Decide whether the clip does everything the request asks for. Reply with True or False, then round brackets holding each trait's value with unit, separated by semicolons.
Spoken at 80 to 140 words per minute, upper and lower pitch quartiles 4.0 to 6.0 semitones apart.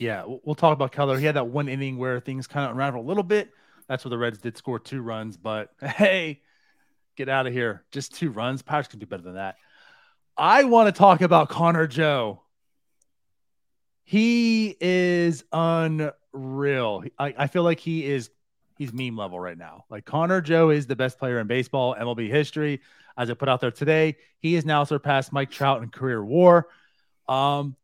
False (190 wpm; 4.8 semitones)